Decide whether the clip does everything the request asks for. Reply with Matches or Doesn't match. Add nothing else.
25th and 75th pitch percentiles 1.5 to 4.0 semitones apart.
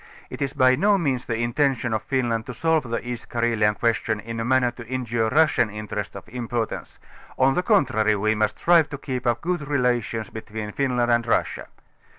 Matches